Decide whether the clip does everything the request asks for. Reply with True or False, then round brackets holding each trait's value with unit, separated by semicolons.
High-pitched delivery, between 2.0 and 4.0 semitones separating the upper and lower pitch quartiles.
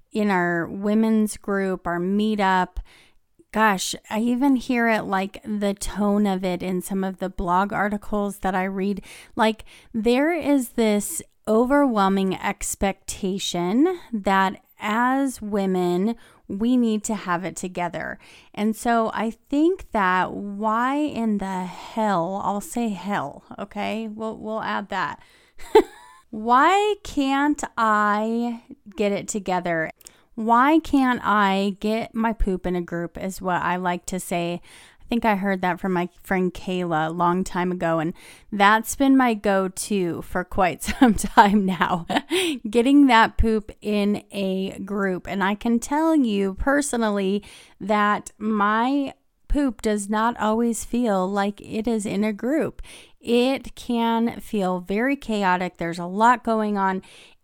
True (210 Hz; 3.7 semitones)